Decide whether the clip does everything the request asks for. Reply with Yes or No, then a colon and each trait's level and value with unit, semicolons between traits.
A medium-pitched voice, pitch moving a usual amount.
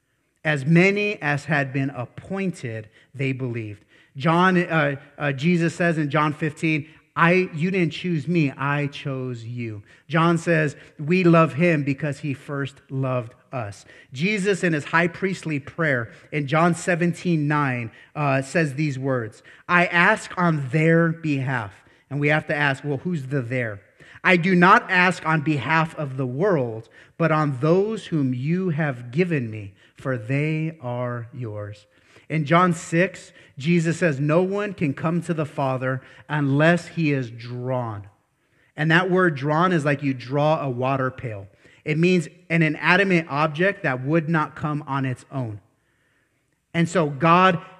Yes: medium, 150 Hz; average, 4.2 semitones